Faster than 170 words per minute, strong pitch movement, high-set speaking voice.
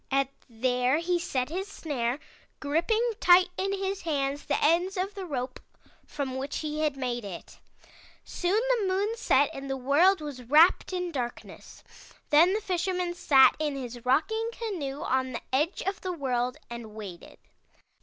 No: average, 165 wpm; wide, 6.1 semitones; very high, 300 Hz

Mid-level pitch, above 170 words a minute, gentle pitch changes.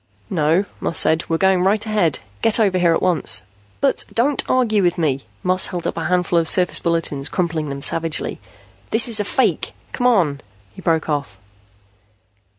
No: medium, 175 Hz; average, 180 wpm; average, 4.3 semitones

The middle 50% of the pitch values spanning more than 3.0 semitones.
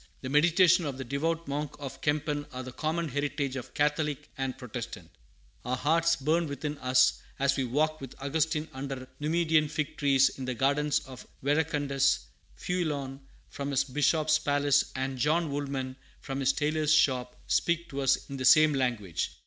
No: narrow, 2.5 semitones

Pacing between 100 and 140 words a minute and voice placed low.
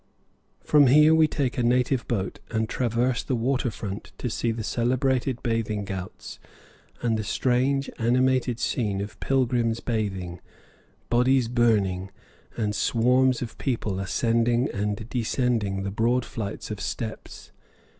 Yes: slow, 135 wpm; low, 115 Hz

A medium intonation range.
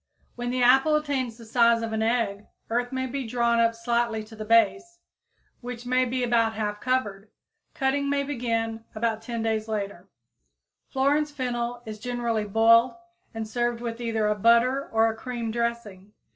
No: narrow, 1.9 semitones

